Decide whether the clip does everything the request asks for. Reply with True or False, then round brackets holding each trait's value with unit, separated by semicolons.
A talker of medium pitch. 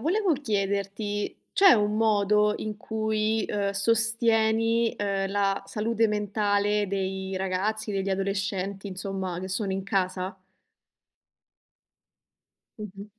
False (205 Hz)